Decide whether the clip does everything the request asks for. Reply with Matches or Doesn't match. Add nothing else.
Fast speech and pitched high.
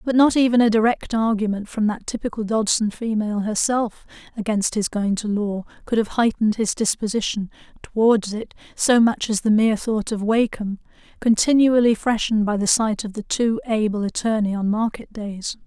Doesn't match